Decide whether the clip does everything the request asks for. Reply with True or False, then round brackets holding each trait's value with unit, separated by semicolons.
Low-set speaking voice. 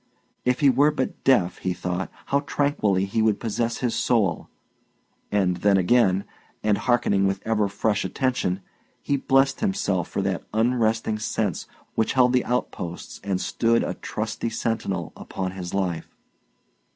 True (110 Hz)